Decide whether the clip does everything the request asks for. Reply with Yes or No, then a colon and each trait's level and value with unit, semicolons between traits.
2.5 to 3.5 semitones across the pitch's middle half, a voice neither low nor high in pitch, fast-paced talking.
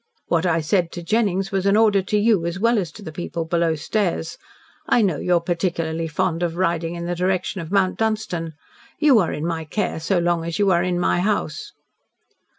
Yes: average, 3.1 semitones; medium, 175 Hz; fast, 215 wpm